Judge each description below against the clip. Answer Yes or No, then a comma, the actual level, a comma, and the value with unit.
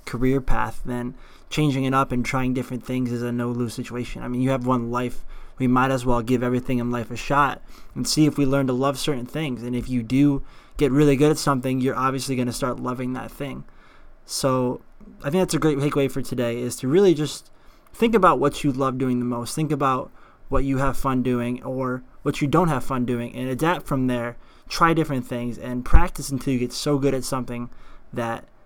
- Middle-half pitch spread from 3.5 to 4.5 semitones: No, narrow, 2.5 semitones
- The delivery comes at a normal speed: No, fast, 230 wpm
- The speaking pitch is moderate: No, low, 130 Hz